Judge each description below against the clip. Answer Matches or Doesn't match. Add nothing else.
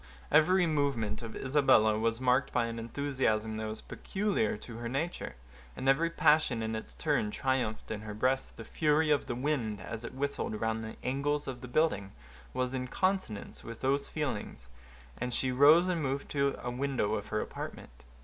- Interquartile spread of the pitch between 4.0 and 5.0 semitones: Matches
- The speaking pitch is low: Matches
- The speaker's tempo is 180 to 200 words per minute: Matches